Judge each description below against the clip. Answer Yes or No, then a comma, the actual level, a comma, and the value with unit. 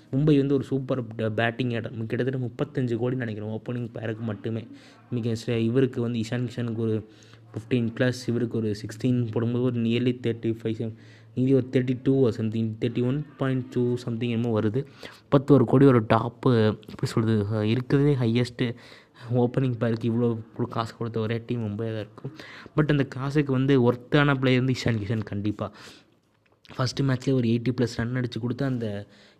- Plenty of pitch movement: No, narrow, 2.5 semitones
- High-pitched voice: No, low, 120 Hz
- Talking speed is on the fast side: Yes, fast, 160 wpm